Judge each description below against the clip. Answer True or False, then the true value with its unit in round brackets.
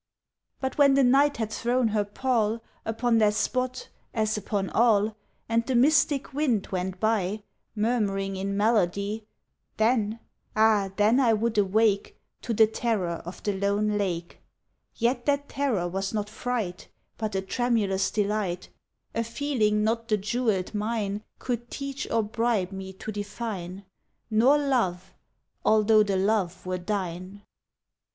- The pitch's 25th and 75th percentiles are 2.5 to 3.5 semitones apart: True (2.9 semitones)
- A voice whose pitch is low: False (215 Hz)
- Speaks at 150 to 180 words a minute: False (140 wpm)